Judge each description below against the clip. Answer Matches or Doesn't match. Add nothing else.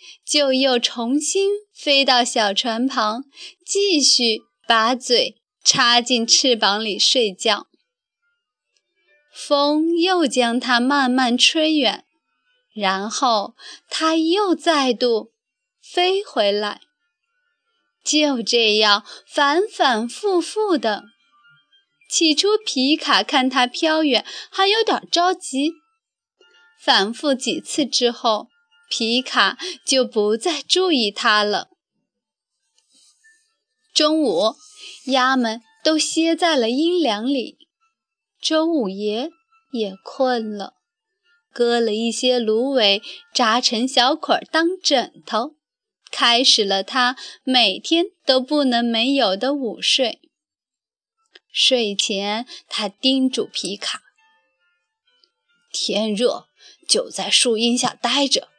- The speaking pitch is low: Doesn't match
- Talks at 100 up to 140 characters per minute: Matches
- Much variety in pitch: Matches